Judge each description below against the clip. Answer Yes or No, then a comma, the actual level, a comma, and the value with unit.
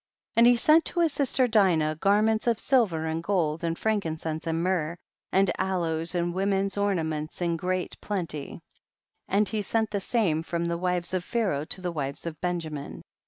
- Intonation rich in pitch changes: No, average, 4.1 semitones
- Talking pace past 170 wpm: Yes, average, 180 wpm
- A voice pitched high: No, medium, 180 Hz